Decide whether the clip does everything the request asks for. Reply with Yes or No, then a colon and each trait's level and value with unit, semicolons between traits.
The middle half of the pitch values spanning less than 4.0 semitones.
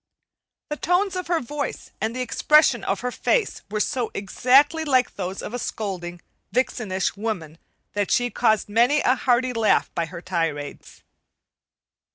No: wide, 5.5 semitones